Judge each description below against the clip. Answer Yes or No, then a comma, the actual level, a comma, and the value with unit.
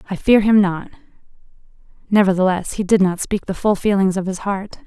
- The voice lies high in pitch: Yes, high, 195 Hz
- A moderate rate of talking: Yes, average, 185 wpm